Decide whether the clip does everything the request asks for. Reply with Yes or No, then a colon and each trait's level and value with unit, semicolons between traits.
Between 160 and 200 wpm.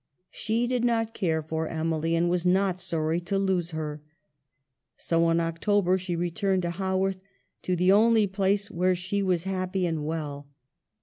Yes: average, 165 wpm